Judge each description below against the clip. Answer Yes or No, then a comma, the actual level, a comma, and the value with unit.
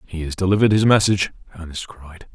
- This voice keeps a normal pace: Yes, average, 180 wpm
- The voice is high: No, very low, 90 Hz